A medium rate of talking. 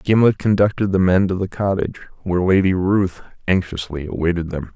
Yes: average, 165 wpm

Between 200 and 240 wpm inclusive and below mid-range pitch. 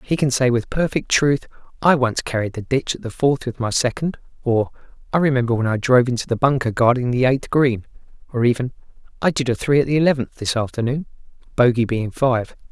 Yes: fast, 205 wpm; low, 125 Hz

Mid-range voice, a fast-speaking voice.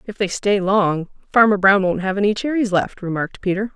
No: high, 200 Hz; fast, 210 wpm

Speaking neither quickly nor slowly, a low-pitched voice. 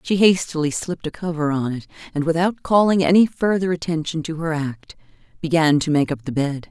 No: average, 195 wpm; medium, 160 Hz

